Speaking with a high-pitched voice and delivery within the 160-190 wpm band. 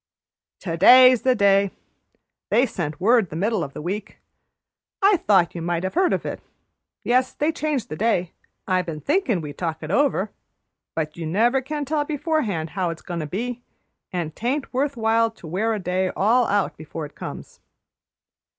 Yes: high, 205 Hz; average, 180 wpm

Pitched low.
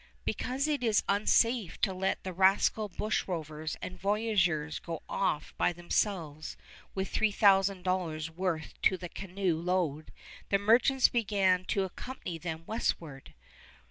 No: high, 190 Hz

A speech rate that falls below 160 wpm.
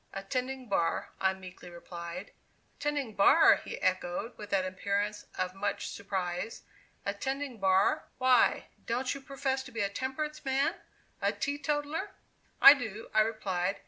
Yes: average, 140 wpm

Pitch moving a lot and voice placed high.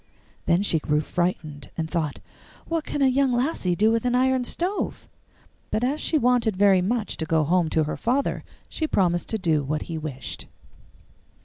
Yes: wide, 7.7 semitones; high, 195 Hz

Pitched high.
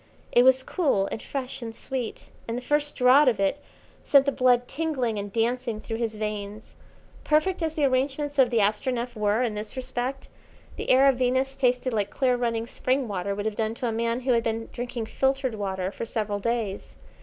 Yes: high, 245 Hz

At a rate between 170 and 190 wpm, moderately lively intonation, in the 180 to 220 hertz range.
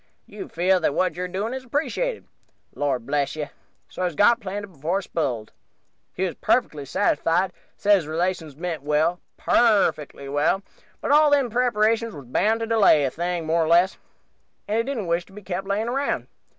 No: average, 185 wpm; wide, 5.9 semitones; medium, 185 Hz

